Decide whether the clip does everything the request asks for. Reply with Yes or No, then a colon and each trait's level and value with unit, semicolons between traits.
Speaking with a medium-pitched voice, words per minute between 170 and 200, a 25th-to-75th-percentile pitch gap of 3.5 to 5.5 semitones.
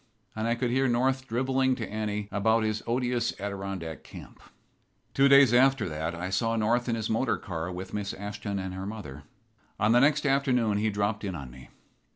No: low, 110 Hz; average, 190 wpm; average, 4.1 semitones